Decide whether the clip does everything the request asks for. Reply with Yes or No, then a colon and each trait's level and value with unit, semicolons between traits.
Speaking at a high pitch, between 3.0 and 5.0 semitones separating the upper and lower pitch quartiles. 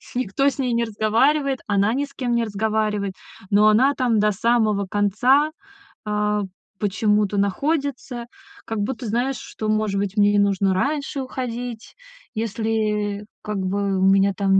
Yes: high, 215 Hz; average, 3.4 semitones